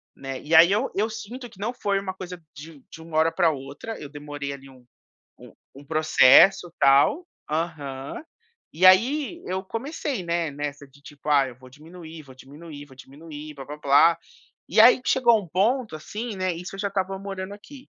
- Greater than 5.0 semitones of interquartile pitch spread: Yes, wide, 5.6 semitones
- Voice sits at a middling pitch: Yes, medium, 165 Hz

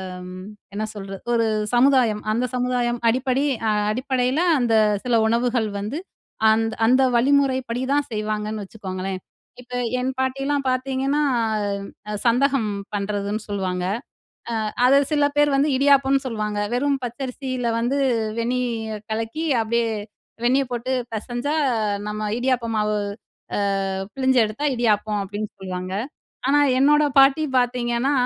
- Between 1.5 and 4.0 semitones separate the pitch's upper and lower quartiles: Yes, average, 3.6 semitones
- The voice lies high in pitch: Yes, high, 245 Hz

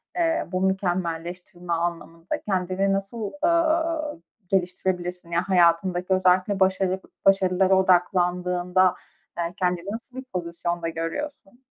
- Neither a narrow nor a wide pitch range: No, narrow, 1.8 semitones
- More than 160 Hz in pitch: Yes, medium, 185 Hz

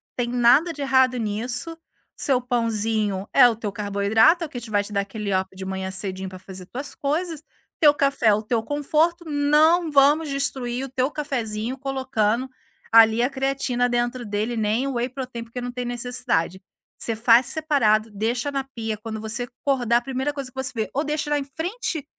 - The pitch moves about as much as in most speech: Yes, average, 4.1 semitones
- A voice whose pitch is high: Yes, high, 245 Hz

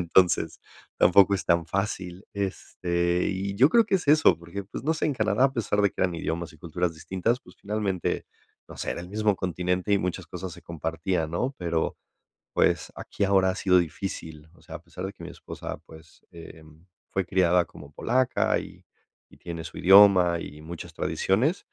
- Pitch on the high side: No, very low, 90 Hz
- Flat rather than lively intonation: No, average, 3.0 semitones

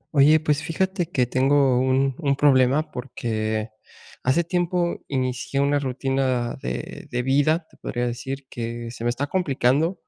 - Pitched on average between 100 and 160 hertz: Yes, low, 135 Hz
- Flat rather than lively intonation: No, average, 3.3 semitones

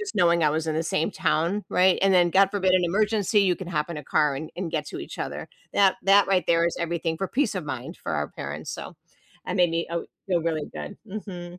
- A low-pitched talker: No, medium, 175 Hz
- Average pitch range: Yes, average, 3.1 semitones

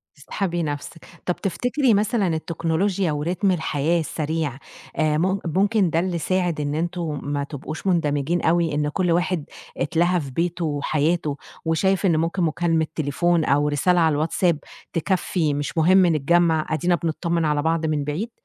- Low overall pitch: No, medium, 165 Hz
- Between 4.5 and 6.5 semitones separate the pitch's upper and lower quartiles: No, average, 2.8 semitones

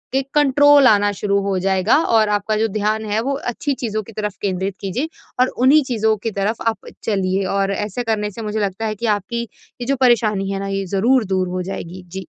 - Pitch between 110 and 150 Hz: No, high, 210 Hz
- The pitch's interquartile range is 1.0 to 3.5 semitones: Yes, average, 3.2 semitones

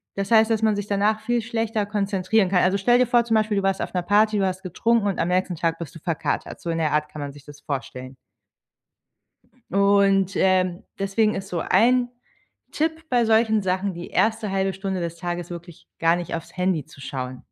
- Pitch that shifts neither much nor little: Yes, average, 3.9 semitones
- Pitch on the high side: Yes, high, 195 Hz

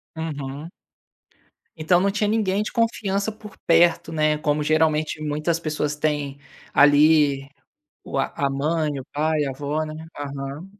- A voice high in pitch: No, medium, 155 Hz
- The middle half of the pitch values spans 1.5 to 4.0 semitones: Yes, narrow, 2.5 semitones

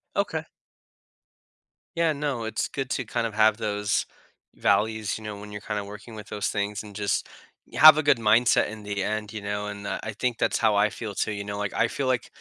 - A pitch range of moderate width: No, narrow, 2.0 semitones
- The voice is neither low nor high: No, low, 105 Hz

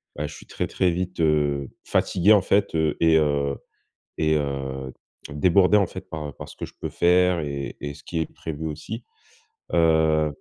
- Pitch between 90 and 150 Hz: No, very low, 80 Hz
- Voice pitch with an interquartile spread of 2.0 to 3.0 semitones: No, average, 3.5 semitones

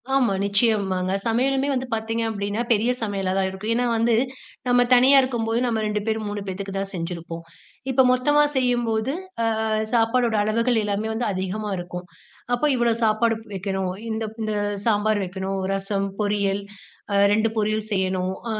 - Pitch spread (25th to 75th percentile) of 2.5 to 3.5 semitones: Yes, average, 3.1 semitones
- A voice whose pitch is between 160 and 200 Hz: No, high, 215 Hz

